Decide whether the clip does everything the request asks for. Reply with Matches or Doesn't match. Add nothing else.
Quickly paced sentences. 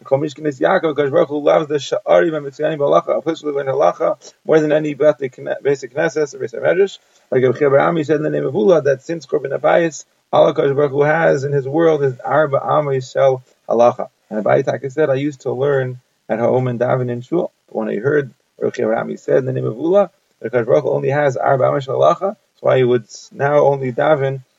Matches